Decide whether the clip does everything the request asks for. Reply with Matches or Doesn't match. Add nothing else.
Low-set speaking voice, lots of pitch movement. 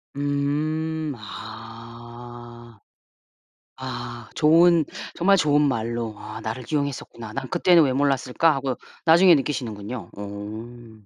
Doesn't match